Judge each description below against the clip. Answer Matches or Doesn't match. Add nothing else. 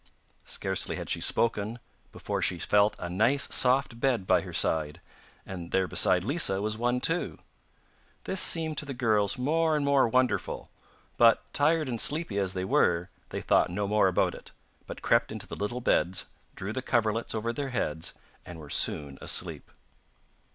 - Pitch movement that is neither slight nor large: Doesn't match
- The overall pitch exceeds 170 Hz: Doesn't match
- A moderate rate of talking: Matches